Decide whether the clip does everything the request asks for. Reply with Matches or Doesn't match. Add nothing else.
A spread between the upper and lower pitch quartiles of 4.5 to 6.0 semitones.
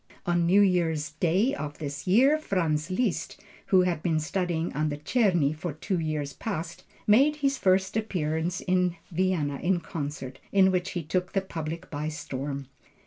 Doesn't match